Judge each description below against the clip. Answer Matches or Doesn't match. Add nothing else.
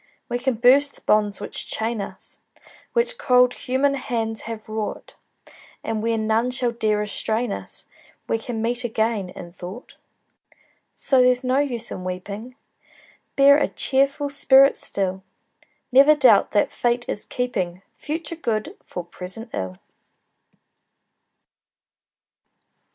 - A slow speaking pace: Matches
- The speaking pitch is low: Doesn't match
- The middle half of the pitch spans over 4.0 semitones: Doesn't match